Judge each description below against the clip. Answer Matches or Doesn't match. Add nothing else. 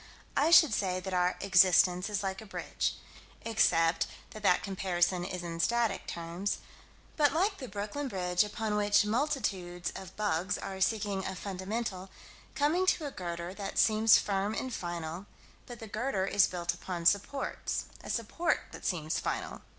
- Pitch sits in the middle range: Doesn't match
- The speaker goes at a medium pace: Matches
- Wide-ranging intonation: Doesn't match